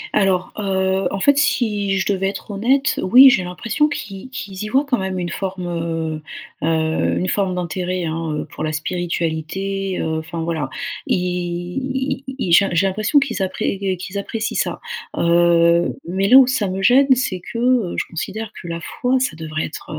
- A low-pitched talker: No, high, 190 Hz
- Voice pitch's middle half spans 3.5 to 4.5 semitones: Yes, average, 4.2 semitones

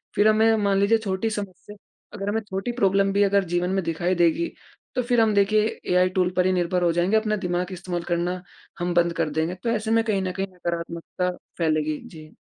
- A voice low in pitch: No, medium, 185 Hz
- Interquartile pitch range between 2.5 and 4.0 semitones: Yes, average, 3.1 semitones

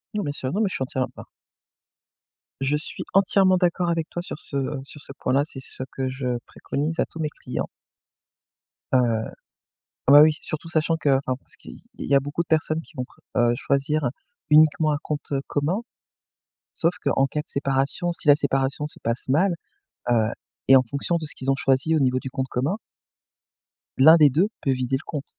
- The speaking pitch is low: No, medium, 145 Hz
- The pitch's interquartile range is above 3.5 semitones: No, average, 3.2 semitones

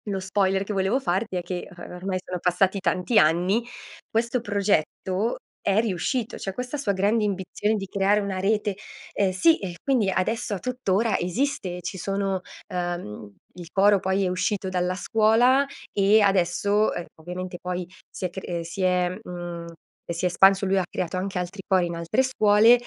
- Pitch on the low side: No, high, 195 Hz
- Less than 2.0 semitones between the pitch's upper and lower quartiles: No, narrow, 2.6 semitones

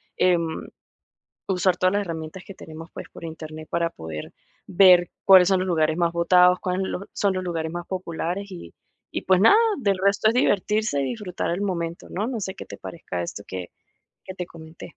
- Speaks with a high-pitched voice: No, medium, 180 Hz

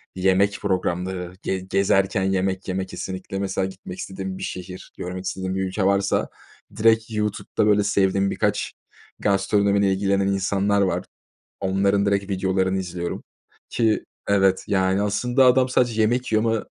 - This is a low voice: Yes, very low, 95 Hz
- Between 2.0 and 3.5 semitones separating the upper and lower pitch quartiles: No, narrow, 1.4 semitones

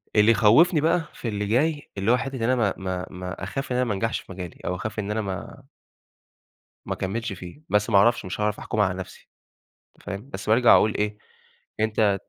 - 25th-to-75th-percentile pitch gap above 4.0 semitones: No, average, 3.7 semitones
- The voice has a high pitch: No, low, 105 Hz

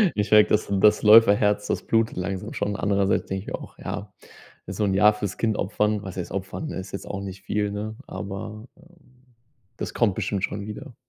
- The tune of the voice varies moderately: No, narrow, 1.6 semitones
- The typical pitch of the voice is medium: No, low, 105 Hz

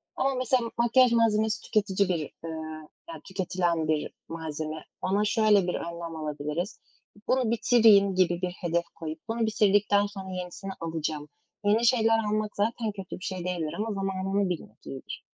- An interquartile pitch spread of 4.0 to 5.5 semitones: Yes, average, 4.5 semitones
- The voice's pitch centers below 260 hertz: Yes, high, 190 Hz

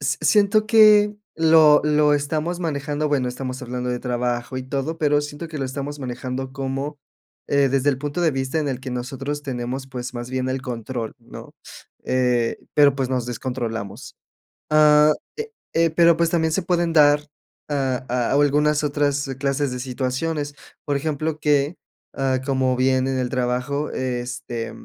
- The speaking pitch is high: No, medium, 140 Hz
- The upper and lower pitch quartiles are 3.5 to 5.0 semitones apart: No, average, 2.9 semitones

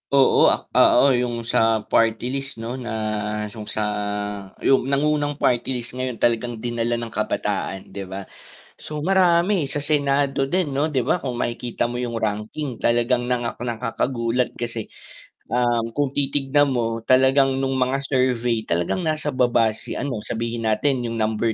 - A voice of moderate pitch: No, low, 125 Hz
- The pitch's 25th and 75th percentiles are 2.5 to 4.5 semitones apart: Yes, average, 3.0 semitones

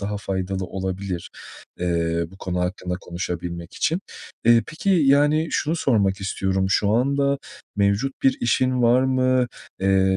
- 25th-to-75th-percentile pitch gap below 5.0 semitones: No, wide, 5.6 semitones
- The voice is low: Yes, low, 100 Hz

